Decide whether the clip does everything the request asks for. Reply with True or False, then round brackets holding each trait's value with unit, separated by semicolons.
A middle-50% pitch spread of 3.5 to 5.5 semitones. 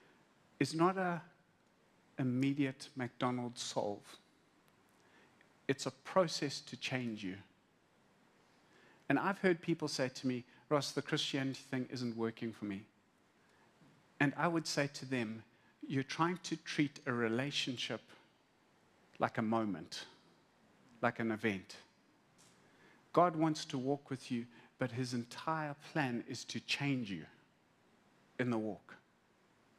True (4.3 semitones)